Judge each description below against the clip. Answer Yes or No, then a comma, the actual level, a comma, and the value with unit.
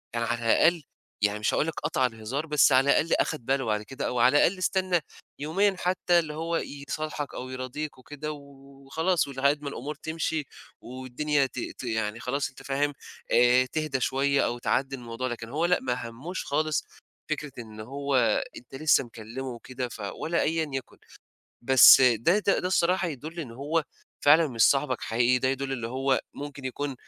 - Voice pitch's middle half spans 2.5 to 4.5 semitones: Yes, average, 3.6 semitones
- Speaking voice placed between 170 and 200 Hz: No, low, 135 Hz